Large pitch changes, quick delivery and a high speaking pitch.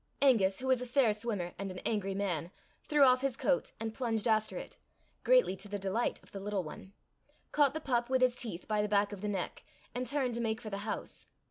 No: average, 4.1 semitones; fast, 235 wpm; high, 220 Hz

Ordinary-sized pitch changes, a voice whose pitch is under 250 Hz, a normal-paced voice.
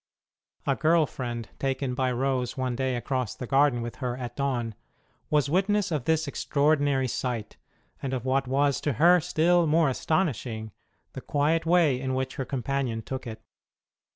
Yes: average, 3.3 semitones; low, 135 Hz; average, 165 wpm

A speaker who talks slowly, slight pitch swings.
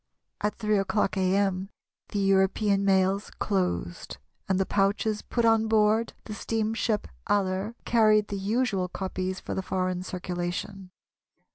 Yes: slow, 130 wpm; narrow, 2.2 semitones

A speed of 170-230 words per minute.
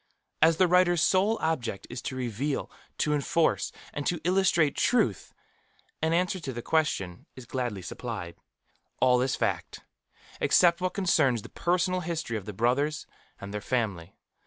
No: average, 155 wpm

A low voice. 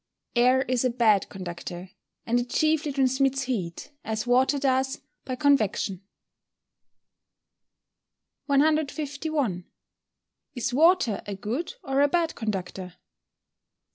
No: very high, 255 Hz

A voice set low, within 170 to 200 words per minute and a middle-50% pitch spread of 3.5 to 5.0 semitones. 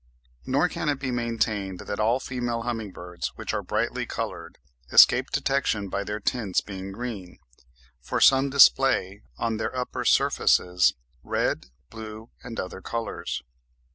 No: low, 115 Hz; average, 140 wpm; average, 4.1 semitones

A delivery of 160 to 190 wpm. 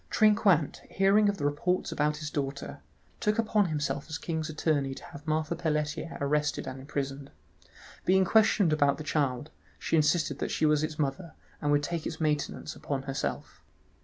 Yes: average, 170 wpm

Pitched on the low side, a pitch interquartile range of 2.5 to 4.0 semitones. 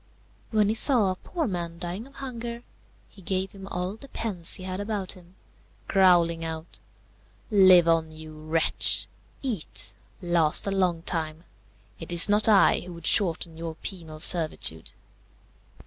No: medium, 180 Hz; average, 3.6 semitones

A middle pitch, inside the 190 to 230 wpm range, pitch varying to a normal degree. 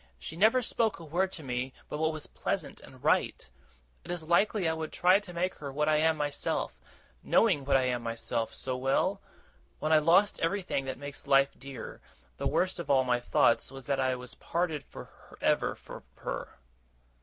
Yes: medium, 150 Hz; average, 195 wpm; average, 4.5 semitones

